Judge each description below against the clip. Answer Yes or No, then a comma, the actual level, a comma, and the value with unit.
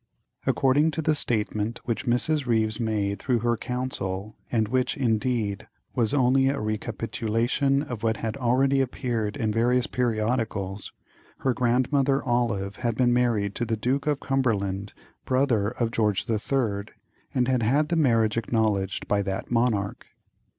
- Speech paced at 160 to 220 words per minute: No, average, 150 wpm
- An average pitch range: Yes, average, 3.2 semitones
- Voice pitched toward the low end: Yes, low, 120 Hz